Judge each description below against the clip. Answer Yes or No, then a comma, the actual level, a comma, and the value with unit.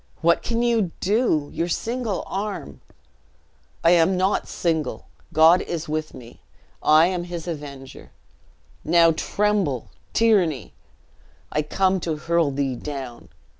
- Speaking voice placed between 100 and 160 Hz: No, medium, 170 Hz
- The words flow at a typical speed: No, slow, 130 wpm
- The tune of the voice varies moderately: Yes, average, 4.1 semitones